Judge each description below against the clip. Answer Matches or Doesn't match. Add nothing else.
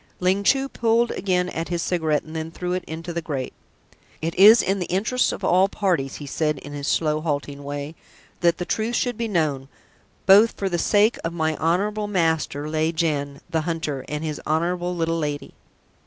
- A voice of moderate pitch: Matches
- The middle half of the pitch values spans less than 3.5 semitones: Doesn't match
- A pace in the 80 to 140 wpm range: Doesn't match